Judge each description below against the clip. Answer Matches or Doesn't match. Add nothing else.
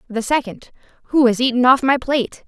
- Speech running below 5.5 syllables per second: Doesn't match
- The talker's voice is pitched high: Matches